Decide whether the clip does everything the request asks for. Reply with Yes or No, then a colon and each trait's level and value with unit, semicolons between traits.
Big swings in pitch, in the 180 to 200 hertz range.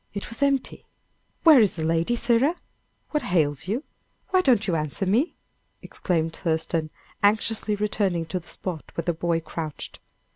Yes: wide, 5.9 semitones; medium, 185 Hz